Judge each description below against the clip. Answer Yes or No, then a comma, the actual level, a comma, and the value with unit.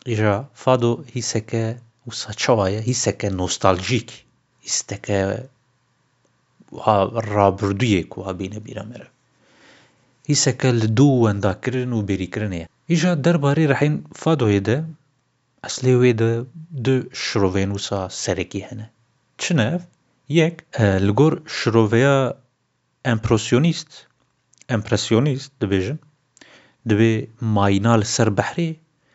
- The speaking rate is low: Yes, slow, 80 wpm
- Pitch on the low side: Yes, low, 120 Hz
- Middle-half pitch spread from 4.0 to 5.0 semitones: Yes, average, 4.5 semitones